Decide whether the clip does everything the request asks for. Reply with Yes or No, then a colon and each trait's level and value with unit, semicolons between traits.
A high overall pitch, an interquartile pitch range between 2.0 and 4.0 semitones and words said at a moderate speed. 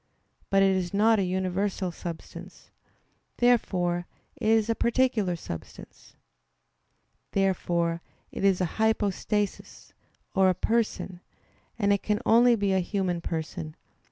No: high, 195 Hz; average, 3.5 semitones; slow, 125 wpm